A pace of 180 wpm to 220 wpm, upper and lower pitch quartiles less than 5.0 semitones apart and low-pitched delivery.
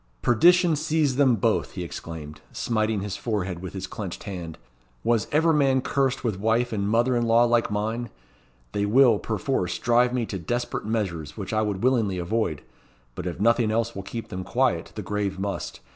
Yes: average, 185 wpm; average, 3.9 semitones; low, 110 Hz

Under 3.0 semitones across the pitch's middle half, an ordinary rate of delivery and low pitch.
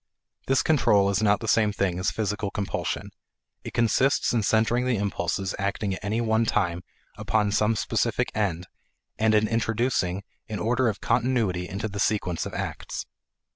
Yes: narrow, 2.5 semitones; average, 165 wpm; low, 105 Hz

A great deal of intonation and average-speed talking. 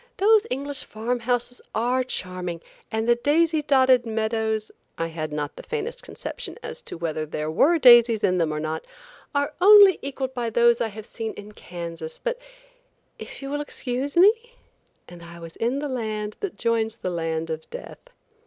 Yes: wide, 7.9 semitones; average, 180 wpm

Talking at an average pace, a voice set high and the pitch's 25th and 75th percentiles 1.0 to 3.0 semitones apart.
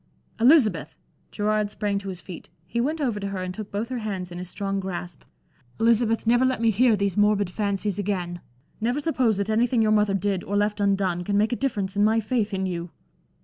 No: fast, 215 wpm; high, 205 Hz; average, 2.7 semitones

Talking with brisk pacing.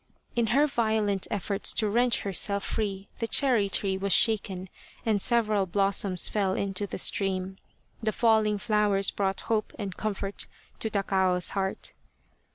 No: average, 145 wpm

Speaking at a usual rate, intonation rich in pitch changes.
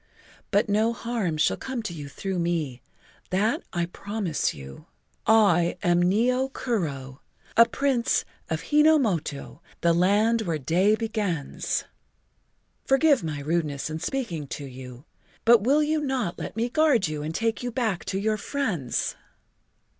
Yes: average, 150 wpm; wide, 6.5 semitones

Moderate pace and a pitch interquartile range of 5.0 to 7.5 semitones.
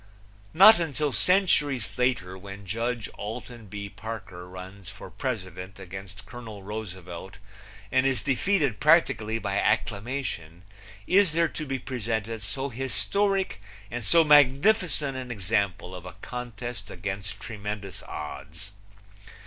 No: slow, 120 wpm; wide, 5.5 semitones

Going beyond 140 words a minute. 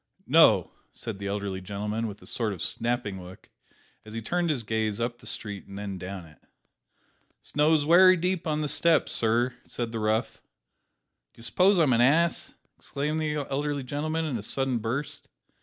Yes: average, 175 wpm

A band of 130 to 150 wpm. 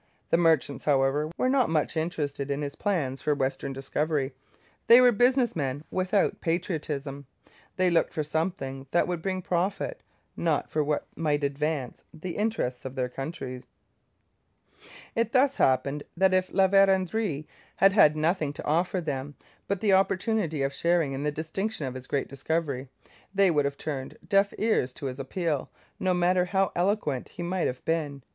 No: average, 165 wpm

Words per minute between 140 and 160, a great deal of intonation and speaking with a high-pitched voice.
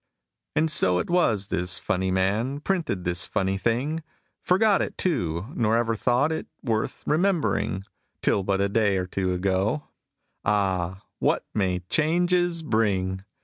No: average, 145 wpm; wide, 8.4 semitones; low, 105 Hz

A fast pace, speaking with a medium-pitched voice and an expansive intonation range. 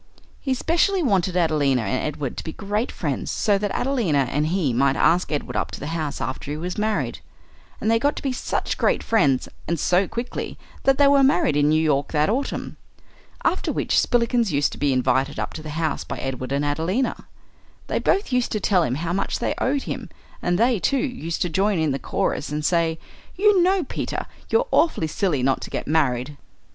Yes: fast, 210 wpm; medium, 170 Hz; wide, 8.4 semitones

